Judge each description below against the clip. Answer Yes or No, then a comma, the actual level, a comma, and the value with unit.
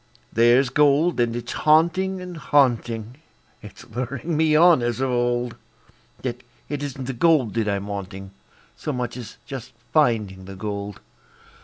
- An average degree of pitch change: Yes, average, 4.7 semitones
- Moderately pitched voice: No, low, 125 Hz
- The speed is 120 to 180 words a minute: Yes, average, 150 wpm